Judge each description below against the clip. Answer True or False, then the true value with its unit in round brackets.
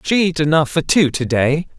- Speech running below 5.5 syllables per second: True (5.0 syllables/s)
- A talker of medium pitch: True (155 Hz)